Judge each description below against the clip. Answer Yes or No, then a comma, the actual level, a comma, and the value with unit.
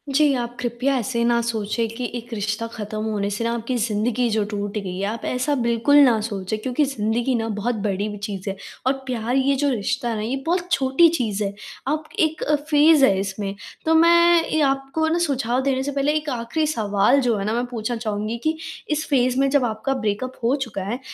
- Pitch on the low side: No, high, 240 Hz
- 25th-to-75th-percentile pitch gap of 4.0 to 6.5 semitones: Yes, average, 4.5 semitones